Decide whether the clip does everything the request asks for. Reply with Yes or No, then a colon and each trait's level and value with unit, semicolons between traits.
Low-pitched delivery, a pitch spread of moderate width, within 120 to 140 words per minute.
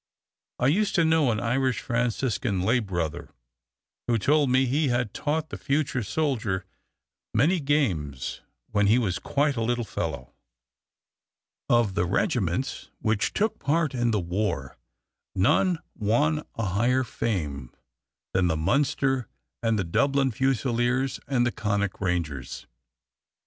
No: low, 120 Hz; wide, 5.7 semitones; slow, 135 wpm